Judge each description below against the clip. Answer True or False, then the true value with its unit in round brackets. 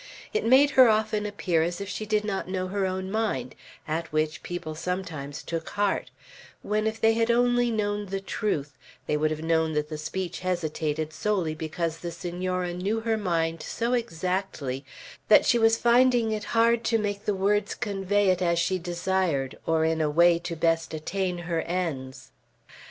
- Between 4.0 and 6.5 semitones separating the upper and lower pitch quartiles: True (4.5 semitones)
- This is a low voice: False (185 Hz)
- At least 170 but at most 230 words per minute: True (180 wpm)